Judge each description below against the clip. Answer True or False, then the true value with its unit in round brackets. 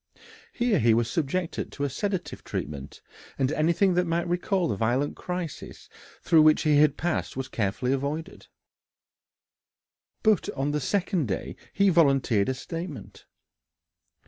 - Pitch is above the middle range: False (155 Hz)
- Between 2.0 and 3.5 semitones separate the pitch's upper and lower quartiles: False (5.1 semitones)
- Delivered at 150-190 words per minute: False (140 wpm)